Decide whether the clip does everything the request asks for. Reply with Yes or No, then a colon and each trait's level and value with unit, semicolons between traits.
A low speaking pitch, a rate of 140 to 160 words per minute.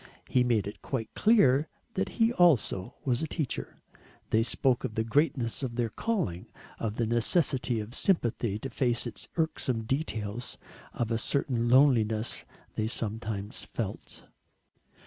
Yes: low, 120 Hz; average, 145 wpm